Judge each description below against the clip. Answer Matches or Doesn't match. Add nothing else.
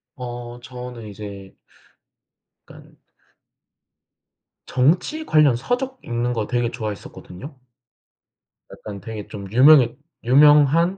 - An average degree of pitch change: Matches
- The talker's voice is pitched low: Matches